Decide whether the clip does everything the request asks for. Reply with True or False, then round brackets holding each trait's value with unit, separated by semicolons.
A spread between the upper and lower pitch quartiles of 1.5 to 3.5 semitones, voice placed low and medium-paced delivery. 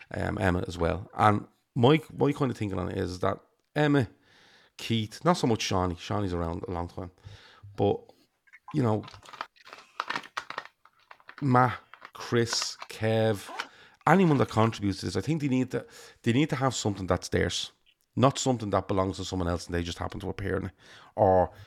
False (4.6 semitones; 105 Hz; 175 wpm)